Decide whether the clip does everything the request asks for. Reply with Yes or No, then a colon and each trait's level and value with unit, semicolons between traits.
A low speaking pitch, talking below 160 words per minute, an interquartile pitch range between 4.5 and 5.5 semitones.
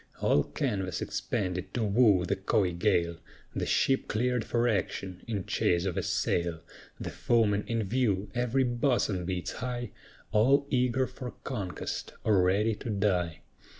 Yes: low, 105 Hz; average, 150 wpm; average, 4.9 semitones